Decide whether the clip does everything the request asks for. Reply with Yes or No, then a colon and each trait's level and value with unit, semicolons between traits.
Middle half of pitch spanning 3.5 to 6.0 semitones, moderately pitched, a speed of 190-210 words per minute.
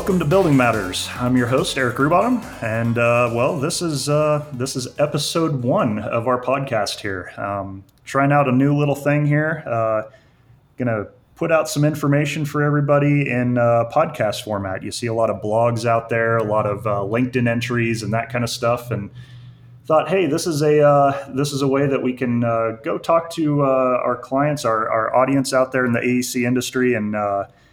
No: average, 3.8 semitones; low, 125 Hz; fast, 205 wpm